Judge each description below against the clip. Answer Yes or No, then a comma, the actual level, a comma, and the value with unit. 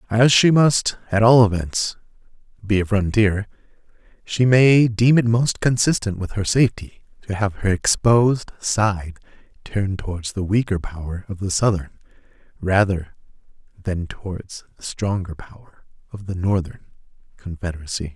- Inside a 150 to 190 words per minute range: No, slow, 135 wpm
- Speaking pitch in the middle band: No, low, 100 Hz